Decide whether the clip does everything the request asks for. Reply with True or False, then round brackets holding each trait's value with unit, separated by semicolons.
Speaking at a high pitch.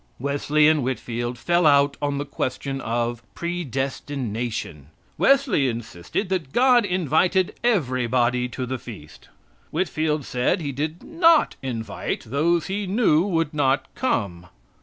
False (140 Hz)